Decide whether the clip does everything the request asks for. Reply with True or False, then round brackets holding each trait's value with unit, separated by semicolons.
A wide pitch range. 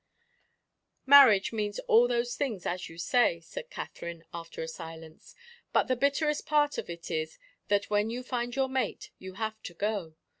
True (6.9 semitones)